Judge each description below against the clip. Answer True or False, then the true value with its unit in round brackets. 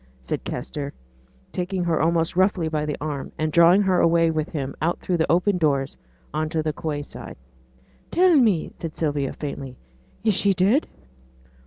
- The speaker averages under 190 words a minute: True (170 wpm)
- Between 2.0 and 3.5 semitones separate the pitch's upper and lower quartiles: True (3.2 semitones)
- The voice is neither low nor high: True (165 Hz)